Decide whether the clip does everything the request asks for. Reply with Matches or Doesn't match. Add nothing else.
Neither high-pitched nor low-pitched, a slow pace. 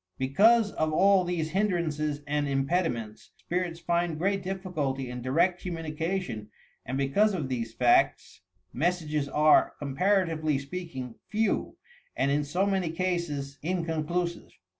Matches